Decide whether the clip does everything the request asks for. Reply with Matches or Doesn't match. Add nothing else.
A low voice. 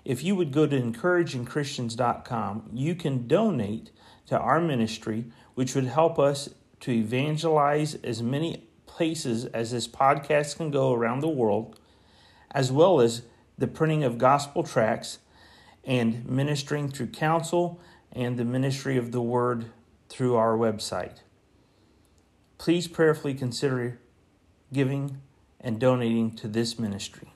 Matches